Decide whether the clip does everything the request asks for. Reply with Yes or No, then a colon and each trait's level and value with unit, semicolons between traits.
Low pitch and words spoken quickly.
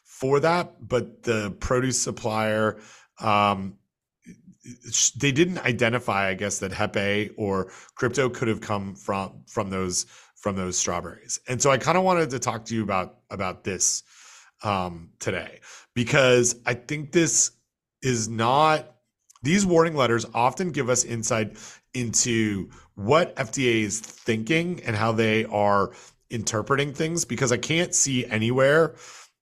No: low, 120 Hz; average, 140 wpm